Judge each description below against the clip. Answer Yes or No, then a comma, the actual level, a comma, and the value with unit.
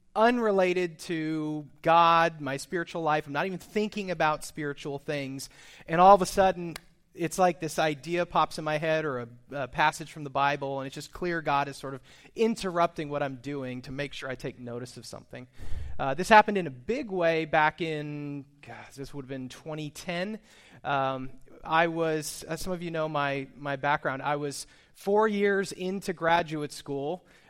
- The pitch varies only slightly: No, average, 3.6 semitones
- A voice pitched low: No, medium, 155 Hz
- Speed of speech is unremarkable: Yes, average, 190 wpm